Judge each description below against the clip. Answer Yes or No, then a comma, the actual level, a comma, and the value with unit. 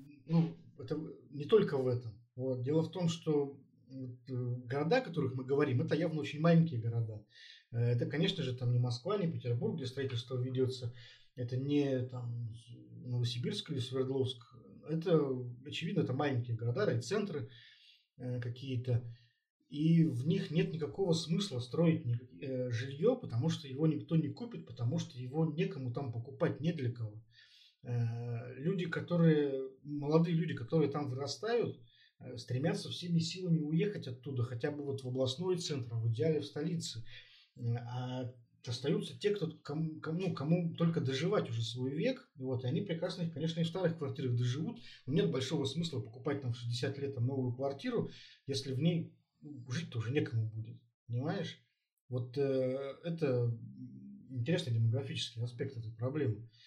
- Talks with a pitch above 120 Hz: Yes, low, 135 Hz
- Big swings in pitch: No, average, 4.5 semitones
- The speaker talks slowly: No, average, 150 wpm